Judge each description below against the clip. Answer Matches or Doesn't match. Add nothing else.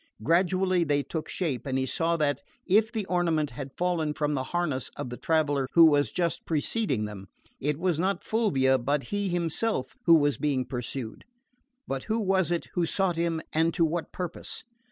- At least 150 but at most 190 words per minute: Matches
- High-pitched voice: Doesn't match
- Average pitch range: Matches